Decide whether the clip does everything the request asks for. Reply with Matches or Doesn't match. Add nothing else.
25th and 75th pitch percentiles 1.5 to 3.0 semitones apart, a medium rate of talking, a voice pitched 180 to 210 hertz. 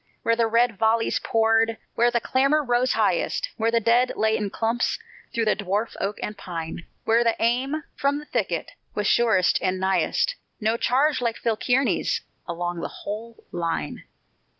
Doesn't match